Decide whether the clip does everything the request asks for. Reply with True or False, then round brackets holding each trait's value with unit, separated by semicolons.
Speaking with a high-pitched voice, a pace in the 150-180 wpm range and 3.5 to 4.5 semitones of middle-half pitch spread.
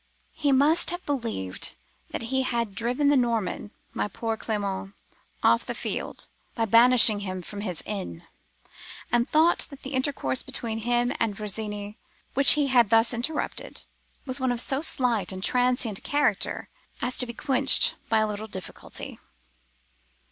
True (235 Hz; 155 wpm; 4.1 semitones)